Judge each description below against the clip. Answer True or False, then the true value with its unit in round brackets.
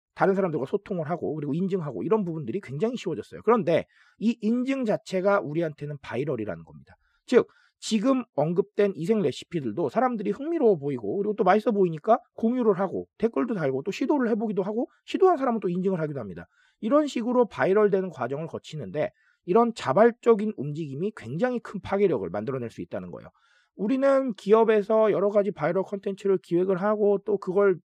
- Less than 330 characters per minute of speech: False (425 characters per minute)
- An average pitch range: True (3.5 semitones)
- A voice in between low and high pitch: False (205 Hz)